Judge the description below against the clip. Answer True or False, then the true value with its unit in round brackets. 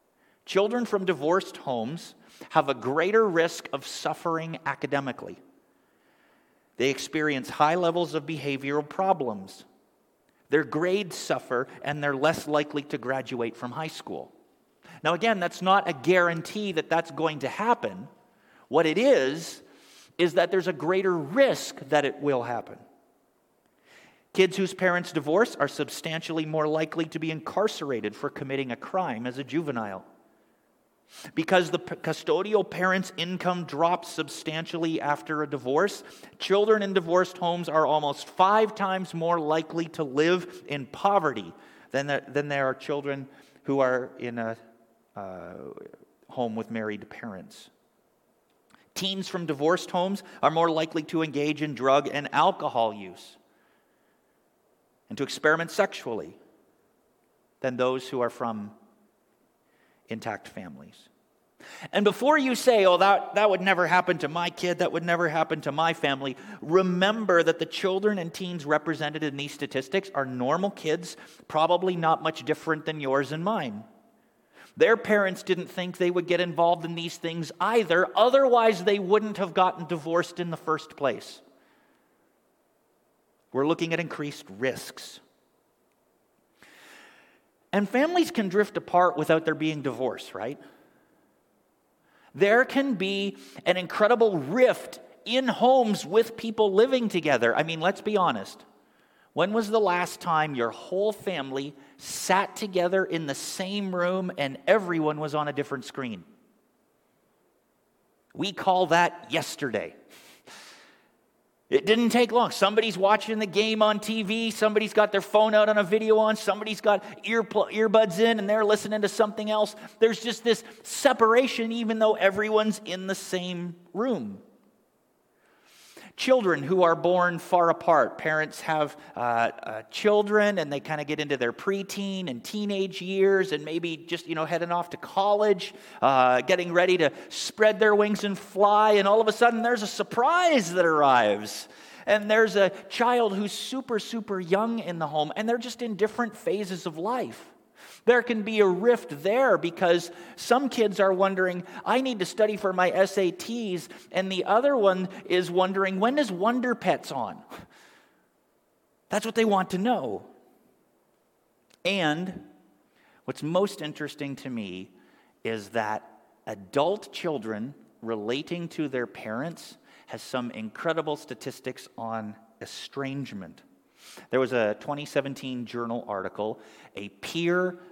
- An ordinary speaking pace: True (145 wpm)